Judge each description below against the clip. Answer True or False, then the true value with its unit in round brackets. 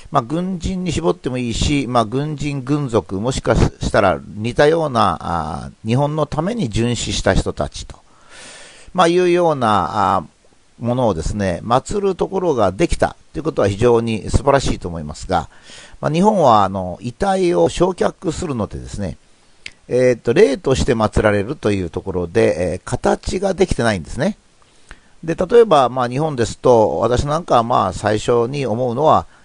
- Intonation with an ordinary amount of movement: False (7.0 semitones)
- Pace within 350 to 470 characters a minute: False (325 characters per minute)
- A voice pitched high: False (125 Hz)